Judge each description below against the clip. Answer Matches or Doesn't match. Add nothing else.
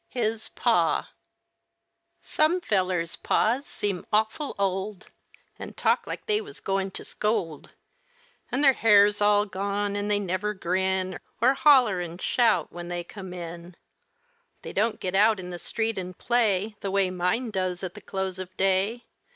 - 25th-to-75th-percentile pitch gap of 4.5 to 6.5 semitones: Doesn't match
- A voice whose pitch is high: Matches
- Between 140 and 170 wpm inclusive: Matches